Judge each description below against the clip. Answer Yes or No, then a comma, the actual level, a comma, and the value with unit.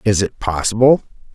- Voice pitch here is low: Yes, low, 105 Hz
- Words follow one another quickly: No, slow, 135 wpm